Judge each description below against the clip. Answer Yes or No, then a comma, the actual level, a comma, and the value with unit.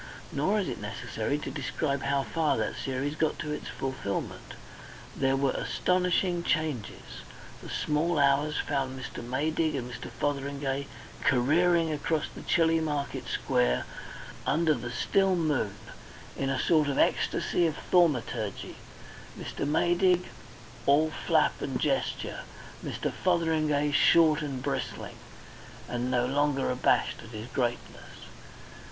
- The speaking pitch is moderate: Yes, medium, 145 Hz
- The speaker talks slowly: Yes, slow, 130 wpm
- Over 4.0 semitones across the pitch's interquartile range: No, average, 3.4 semitones